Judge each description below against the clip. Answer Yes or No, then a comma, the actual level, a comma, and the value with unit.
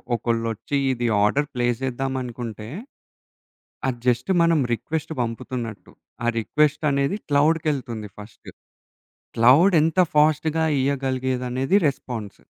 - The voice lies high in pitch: No, low, 130 Hz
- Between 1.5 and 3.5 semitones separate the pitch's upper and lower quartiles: No, average, 4.0 semitones